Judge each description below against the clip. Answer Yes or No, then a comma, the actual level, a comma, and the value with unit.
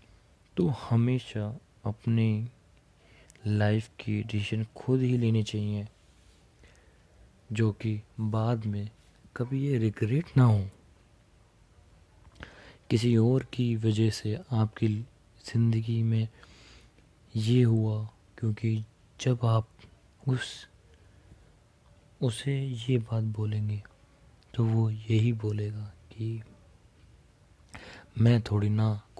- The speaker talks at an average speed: No, slow, 90 wpm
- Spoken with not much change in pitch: Yes, narrow, 2.0 semitones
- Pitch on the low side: Yes, low, 110 Hz